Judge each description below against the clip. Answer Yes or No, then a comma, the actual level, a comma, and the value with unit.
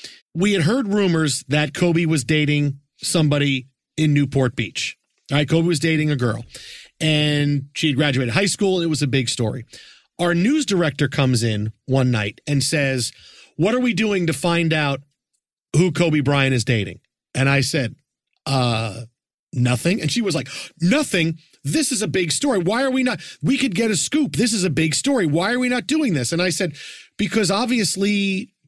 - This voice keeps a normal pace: Yes, average, 190 wpm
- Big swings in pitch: Yes, wide, 5.9 semitones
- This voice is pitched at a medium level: Yes, medium, 155 Hz